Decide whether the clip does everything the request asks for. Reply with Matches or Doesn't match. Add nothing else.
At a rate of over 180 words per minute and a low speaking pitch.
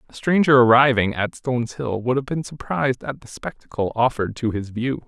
Matches